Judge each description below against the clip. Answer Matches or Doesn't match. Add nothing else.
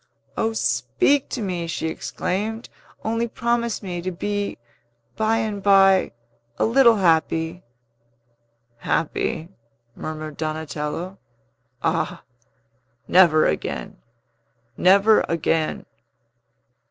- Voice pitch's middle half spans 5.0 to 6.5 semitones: Matches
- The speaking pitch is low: Doesn't match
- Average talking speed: Doesn't match